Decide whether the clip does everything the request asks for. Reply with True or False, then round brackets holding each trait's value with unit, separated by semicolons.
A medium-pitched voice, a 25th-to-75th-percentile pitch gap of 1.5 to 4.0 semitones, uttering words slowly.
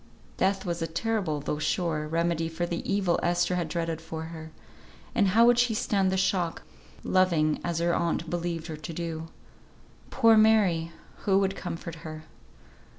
False (170 Hz; 2.9 semitones; 165 wpm)